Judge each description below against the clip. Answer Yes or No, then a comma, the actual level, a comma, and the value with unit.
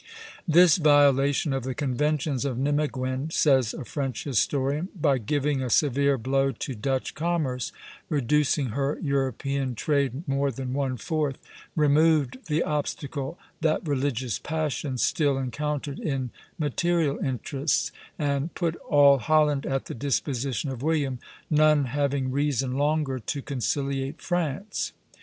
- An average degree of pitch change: No, narrow, 2.2 semitones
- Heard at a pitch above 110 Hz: Yes, medium, 140 Hz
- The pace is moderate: No, slow, 130 wpm